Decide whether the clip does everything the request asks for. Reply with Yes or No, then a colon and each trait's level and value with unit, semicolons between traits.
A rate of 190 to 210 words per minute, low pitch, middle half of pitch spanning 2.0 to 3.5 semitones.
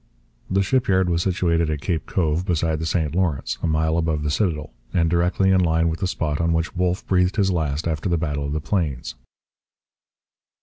Yes: average, 200 wpm; very low, 85 Hz; average, 2.7 semitones